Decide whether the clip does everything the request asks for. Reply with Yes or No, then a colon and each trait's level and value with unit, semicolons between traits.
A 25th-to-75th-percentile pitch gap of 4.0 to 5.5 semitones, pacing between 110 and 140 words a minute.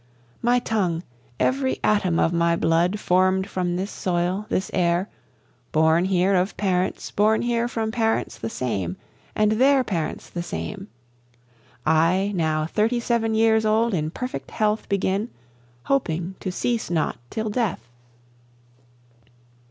Yes: average, 4.4 semitones; slow, 135 wpm